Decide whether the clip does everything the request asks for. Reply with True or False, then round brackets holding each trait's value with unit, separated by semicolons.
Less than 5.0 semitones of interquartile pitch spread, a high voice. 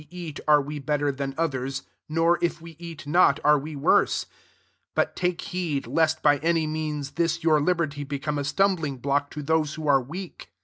False (2.6 semitones; 150 Hz)